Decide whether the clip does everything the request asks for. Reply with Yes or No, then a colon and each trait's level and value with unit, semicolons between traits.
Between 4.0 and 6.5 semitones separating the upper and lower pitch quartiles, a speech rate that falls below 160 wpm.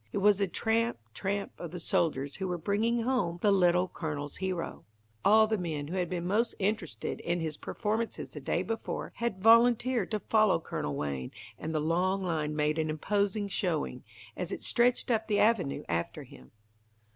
No: average, 5.2 semitones; average, 180 wpm